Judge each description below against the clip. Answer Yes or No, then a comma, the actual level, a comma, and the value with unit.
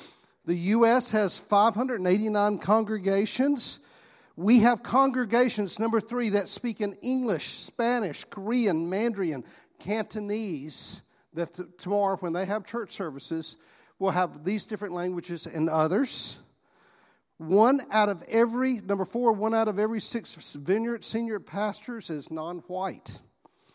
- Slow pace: Yes, slow, 125 wpm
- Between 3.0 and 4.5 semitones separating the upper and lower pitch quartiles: Yes, average, 4.1 semitones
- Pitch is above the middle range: Yes, high, 205 Hz